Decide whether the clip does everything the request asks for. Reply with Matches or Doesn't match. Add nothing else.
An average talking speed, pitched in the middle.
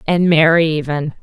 Matches